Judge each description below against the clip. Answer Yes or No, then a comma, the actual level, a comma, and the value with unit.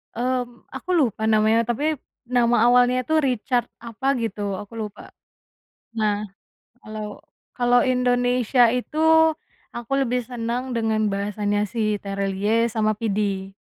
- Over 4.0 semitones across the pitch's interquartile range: No, average, 2.7 semitones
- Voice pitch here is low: No, high, 230 Hz